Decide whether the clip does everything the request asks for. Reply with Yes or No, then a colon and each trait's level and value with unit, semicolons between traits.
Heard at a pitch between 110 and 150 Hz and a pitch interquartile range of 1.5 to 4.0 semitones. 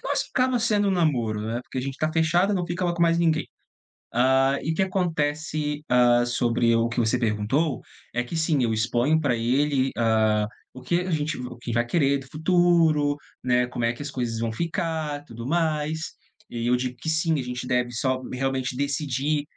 No: low, 135 Hz; average, 4.7 semitones